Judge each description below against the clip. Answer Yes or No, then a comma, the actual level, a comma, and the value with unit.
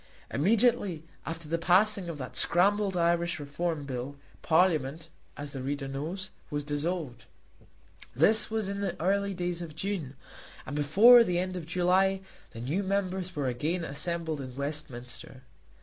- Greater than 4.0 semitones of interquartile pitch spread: Yes, average, 4.6 semitones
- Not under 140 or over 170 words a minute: Yes, average, 150 wpm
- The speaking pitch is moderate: Yes, medium, 170 Hz